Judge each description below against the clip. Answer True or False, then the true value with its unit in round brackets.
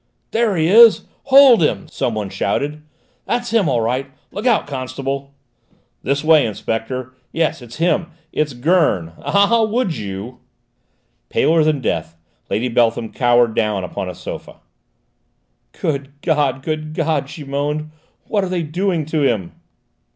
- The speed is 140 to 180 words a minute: True (145 wpm)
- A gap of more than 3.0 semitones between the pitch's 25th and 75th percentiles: True (5.6 semitones)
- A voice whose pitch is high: False (145 Hz)